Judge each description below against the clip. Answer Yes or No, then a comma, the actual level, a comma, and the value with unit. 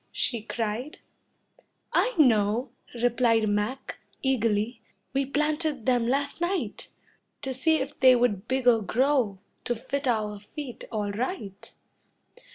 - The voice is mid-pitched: No, high, 245 Hz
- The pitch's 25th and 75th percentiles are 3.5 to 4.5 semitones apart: Yes, average, 3.9 semitones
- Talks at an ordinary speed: No, slow, 120 wpm